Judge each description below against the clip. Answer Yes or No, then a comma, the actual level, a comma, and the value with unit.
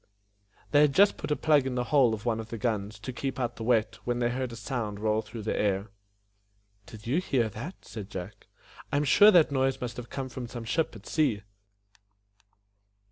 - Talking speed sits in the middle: No, fast, 215 wpm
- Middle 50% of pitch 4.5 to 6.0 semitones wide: No, average, 3.6 semitones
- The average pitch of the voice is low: Yes, low, 120 Hz